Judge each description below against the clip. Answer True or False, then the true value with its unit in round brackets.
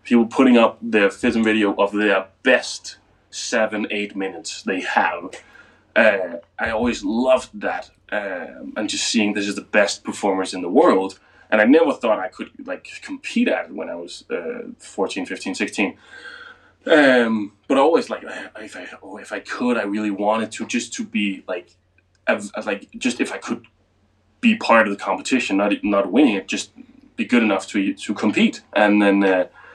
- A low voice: True (110 Hz)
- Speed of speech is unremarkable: True (185 wpm)